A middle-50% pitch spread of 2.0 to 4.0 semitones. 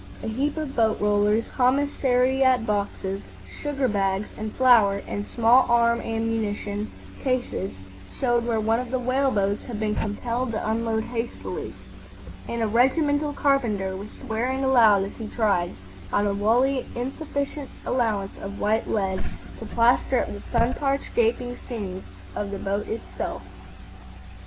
Yes: average, 3.6 semitones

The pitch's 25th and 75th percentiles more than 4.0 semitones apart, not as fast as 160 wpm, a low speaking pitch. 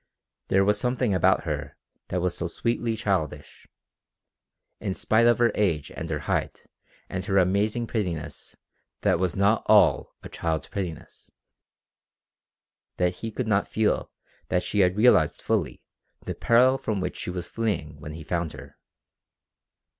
Yes: average, 4.5 semitones; average, 150 wpm; very low, 95 Hz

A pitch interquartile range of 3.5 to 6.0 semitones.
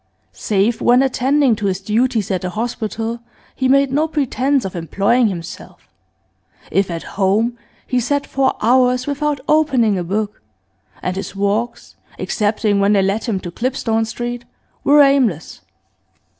Yes: average, 4.6 semitones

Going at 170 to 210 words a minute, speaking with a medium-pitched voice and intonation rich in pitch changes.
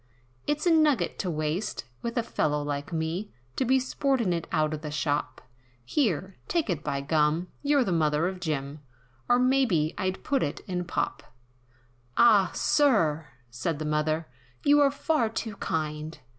No: average, 160 wpm; medium, 175 Hz; wide, 8.1 semitones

